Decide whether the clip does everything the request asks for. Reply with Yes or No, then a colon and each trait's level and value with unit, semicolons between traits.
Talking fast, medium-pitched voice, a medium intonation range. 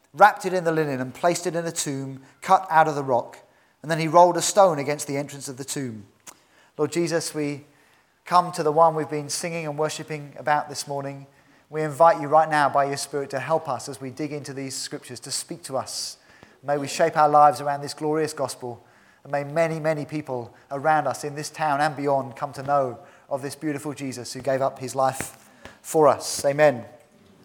No: fast, 220 wpm; medium, 145 Hz; narrow, 2.3 semitones